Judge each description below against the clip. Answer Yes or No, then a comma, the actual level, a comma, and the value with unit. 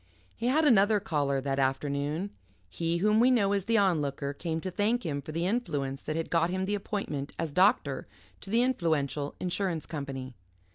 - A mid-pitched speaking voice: Yes, medium, 170 Hz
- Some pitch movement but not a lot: No, wide, 6.2 semitones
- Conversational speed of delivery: Yes, average, 185 wpm